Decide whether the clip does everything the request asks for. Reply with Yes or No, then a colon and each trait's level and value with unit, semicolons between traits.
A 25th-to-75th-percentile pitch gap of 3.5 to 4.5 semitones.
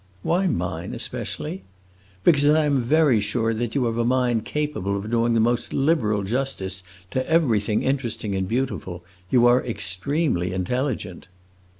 No: average, 4.9 semitones